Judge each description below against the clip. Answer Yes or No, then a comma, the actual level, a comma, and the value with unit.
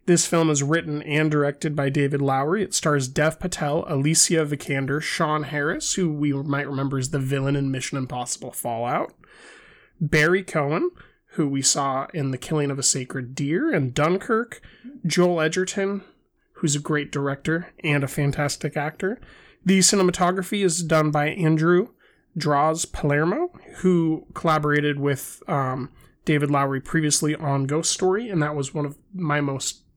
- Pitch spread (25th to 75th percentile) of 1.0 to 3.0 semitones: No, average, 3.5 semitones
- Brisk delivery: No, average, 155 wpm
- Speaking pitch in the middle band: Yes, medium, 150 Hz